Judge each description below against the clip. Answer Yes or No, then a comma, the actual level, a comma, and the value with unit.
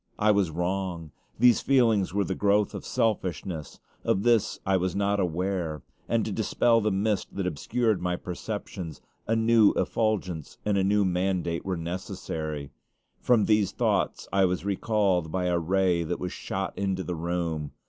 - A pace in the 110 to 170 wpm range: Yes, average, 165 wpm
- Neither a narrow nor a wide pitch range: Yes, average, 3.0 semitones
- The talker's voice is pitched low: Yes, very low, 95 Hz